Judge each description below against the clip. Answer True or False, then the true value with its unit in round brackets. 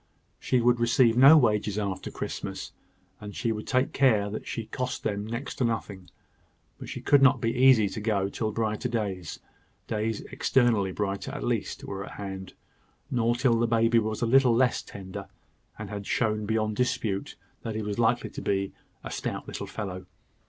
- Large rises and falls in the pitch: False (2.8 semitones)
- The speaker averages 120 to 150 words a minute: False (180 wpm)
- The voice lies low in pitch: True (110 Hz)